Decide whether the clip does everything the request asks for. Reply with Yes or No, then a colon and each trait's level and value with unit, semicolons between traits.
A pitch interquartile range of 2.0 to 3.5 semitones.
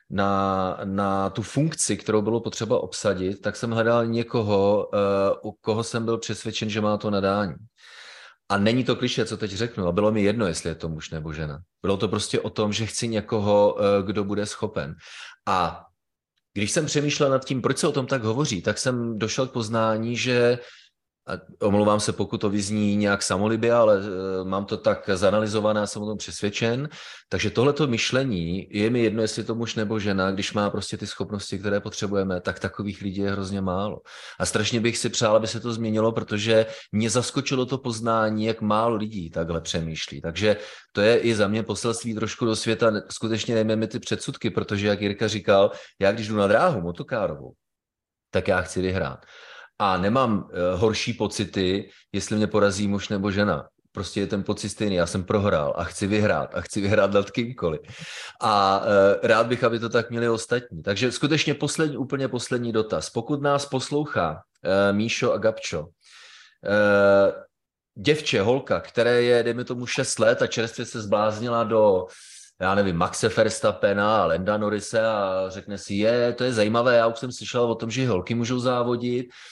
Yes: narrow, 2.6 semitones